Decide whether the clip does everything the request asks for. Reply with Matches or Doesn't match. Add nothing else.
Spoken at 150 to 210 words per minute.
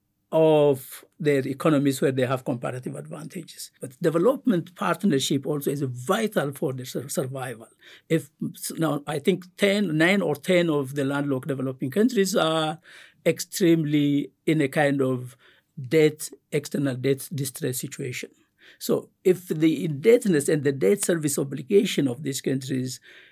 Doesn't match